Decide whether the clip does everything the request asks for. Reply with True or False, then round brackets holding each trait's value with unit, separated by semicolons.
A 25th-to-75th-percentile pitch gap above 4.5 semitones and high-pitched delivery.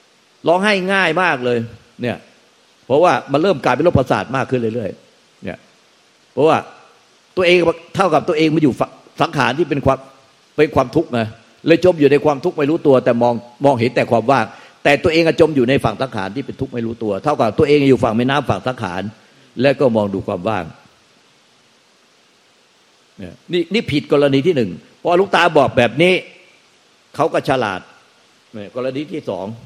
False (5.0 semitones; 135 Hz)